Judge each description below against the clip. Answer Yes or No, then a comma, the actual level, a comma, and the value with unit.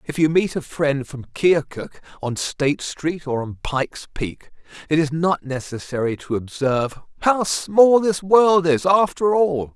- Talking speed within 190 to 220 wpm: No, average, 165 wpm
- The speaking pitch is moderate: Yes, medium, 155 Hz